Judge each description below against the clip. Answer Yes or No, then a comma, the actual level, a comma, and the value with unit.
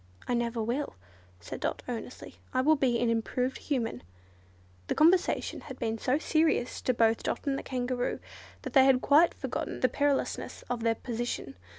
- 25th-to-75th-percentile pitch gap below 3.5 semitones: Yes, average, 3.1 semitones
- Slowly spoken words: No, average, 175 wpm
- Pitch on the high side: Yes, very high, 250 Hz